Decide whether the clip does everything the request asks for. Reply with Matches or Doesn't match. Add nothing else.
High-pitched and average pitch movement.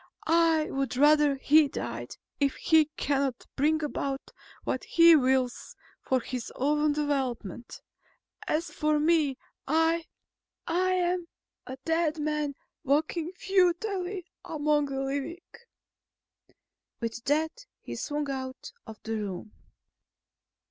Matches